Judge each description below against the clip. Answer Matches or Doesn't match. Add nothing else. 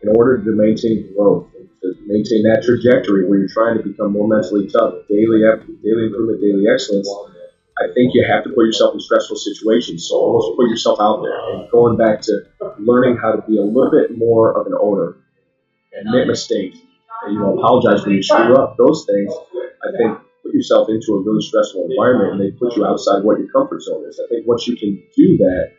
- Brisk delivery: Matches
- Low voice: Matches